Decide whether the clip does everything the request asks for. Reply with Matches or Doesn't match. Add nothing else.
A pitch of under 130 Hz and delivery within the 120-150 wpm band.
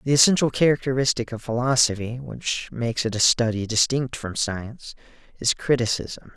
Matches